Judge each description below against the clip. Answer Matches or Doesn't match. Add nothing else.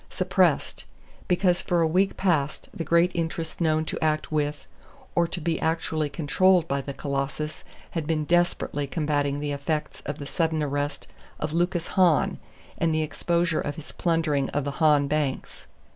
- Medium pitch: Matches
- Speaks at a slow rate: Doesn't match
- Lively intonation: Doesn't match